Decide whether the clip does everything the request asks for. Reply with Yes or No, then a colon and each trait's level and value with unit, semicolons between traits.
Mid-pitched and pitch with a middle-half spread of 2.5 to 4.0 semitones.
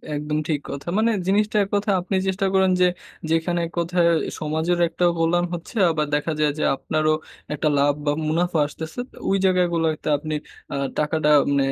Yes: medium, 165 Hz; average, 2.9 semitones